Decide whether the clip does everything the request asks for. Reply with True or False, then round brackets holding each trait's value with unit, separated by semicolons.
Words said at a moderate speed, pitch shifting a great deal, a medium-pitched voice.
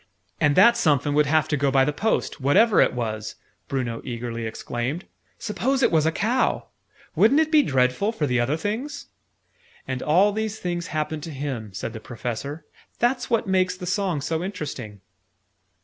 True (180 wpm; 8.1 semitones; 155 Hz)